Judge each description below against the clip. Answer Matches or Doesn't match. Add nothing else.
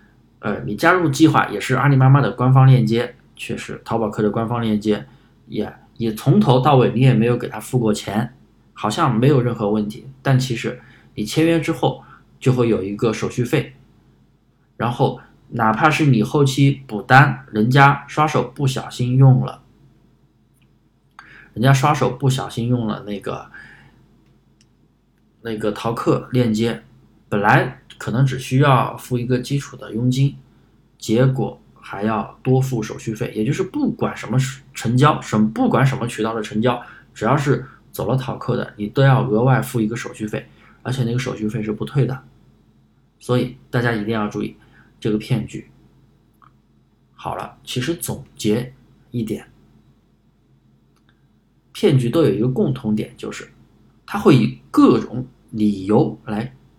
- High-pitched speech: Doesn't match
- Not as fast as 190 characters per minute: Doesn't match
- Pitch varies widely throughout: Doesn't match